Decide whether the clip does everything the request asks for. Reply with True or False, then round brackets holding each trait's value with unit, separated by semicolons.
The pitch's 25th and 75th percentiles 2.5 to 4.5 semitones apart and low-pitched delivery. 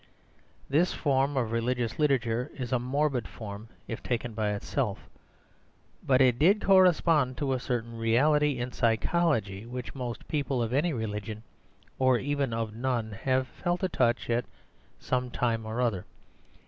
True (3.5 semitones; 125 Hz)